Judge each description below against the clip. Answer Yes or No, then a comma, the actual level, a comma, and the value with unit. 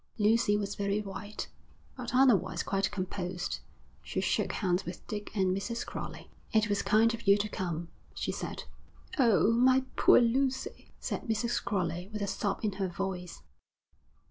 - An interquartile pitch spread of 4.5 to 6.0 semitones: No, average, 3.3 semitones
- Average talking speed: Yes, average, 160 wpm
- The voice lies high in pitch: Yes, high, 205 Hz